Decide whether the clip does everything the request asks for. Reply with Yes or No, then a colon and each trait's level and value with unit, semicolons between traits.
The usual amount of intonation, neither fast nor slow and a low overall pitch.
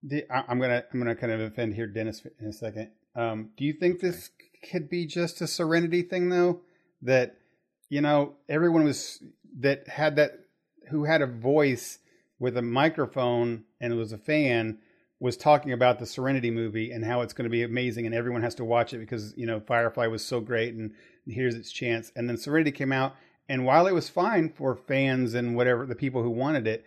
No: average, 4.1 semitones; fast, 210 wpm; low, 125 Hz